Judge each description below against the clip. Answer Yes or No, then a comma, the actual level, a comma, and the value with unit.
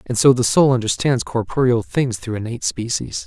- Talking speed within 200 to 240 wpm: No, average, 185 wpm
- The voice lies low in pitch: Yes, low, 120 Hz